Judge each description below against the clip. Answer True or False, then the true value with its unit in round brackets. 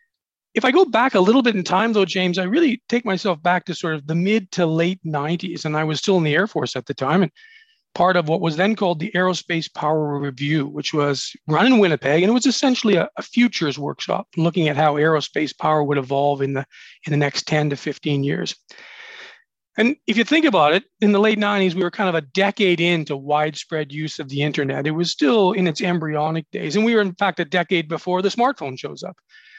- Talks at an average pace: False (235 wpm)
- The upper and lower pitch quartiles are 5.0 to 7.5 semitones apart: True (5.4 semitones)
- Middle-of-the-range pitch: True (175 Hz)